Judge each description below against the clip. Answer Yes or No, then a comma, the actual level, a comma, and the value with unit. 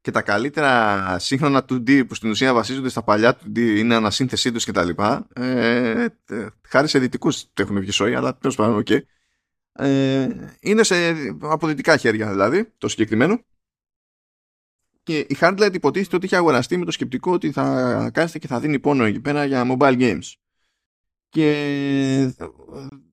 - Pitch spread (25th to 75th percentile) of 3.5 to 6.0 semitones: Yes, average, 4.3 semitones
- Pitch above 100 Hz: Yes, low, 135 Hz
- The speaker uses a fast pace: No, average, 155 wpm